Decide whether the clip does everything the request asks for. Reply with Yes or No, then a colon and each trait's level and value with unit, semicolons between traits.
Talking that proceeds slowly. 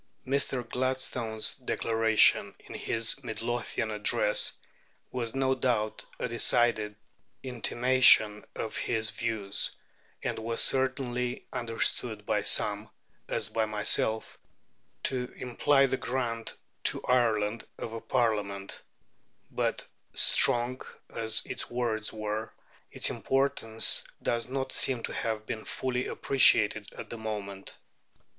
Yes: slow, 110 wpm